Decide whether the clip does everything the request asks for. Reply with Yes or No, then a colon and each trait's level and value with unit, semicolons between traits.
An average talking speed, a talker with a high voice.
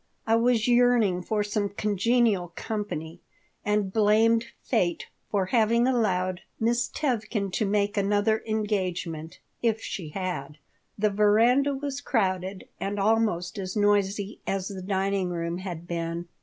No: slow, 130 wpm; high, 205 Hz